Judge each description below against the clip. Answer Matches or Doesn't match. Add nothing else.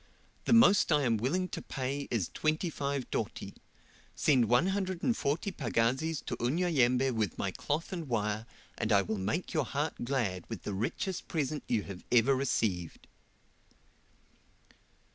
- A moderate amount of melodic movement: Doesn't match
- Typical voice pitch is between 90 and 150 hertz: Matches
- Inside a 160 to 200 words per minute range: Doesn't match